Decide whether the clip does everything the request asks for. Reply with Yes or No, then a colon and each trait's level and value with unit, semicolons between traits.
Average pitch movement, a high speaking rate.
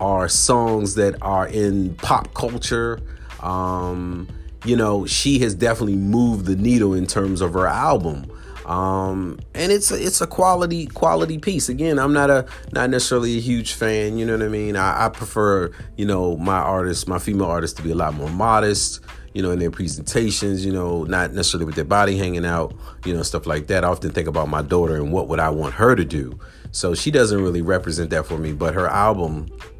Yes: average, 4.7 semitones; fast, 210 wpm